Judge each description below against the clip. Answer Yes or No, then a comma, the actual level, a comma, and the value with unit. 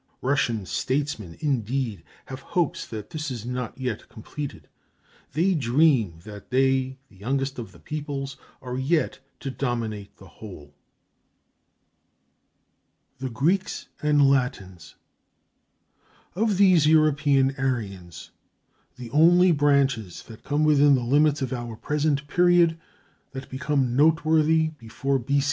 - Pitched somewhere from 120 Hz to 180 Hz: Yes, low, 135 Hz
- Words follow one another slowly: Yes, slow, 120 wpm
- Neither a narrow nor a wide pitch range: Yes, average, 4.1 semitones